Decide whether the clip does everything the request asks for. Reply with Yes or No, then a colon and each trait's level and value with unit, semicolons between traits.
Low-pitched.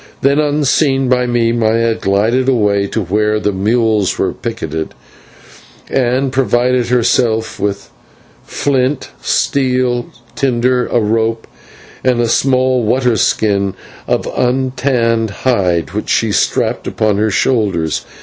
Yes: low, 115 Hz